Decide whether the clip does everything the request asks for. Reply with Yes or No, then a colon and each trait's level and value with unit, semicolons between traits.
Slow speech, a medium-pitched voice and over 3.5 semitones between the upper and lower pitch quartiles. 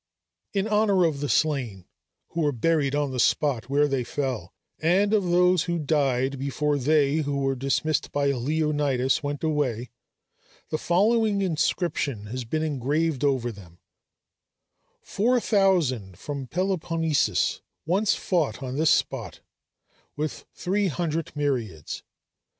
Yes: slow, 130 wpm; medium, 150 Hz; average, 4.2 semitones